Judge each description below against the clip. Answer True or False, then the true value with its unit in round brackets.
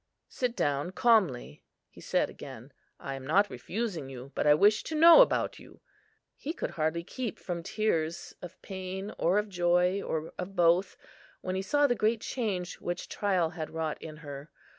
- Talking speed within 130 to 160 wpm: False (180 wpm)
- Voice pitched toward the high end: False (180 Hz)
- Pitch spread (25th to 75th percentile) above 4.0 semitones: True (4.8 semitones)